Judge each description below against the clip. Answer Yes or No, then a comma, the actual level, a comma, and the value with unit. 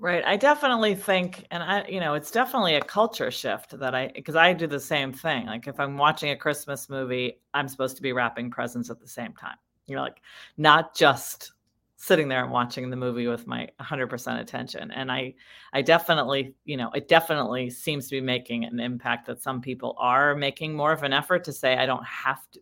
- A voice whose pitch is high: No, medium, 140 Hz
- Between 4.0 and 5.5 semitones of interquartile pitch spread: Yes, average, 4.3 semitones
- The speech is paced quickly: Yes, fast, 220 wpm